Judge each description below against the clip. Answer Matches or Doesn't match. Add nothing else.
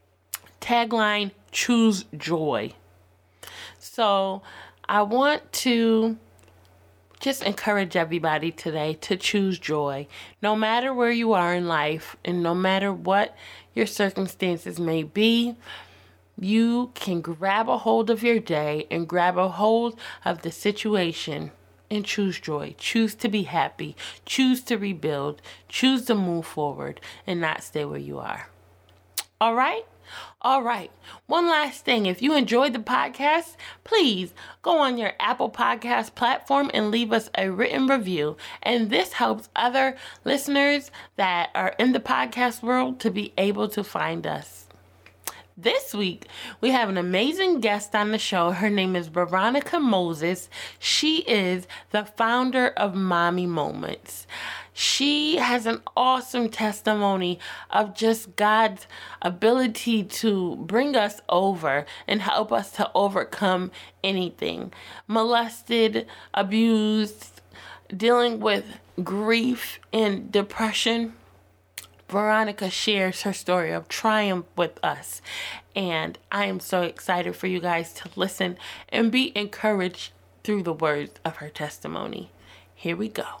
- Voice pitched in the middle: Doesn't match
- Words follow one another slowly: Matches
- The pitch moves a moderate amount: Matches